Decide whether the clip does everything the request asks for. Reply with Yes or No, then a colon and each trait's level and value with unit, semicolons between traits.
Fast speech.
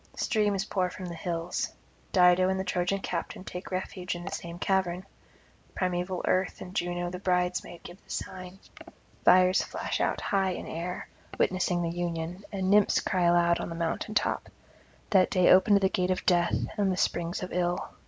No: average, 180 wpm